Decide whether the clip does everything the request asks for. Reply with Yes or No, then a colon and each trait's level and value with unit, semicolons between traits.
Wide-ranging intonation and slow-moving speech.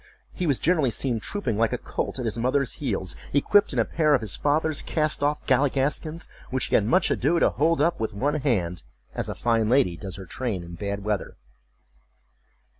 No: wide, 6.0 semitones; average, 200 wpm